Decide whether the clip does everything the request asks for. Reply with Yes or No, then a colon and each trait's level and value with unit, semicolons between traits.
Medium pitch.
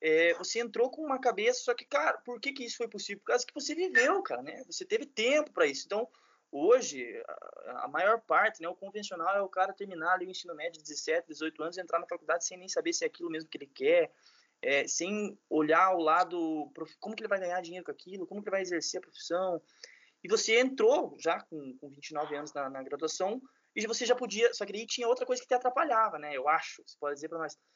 No: high, 200 Hz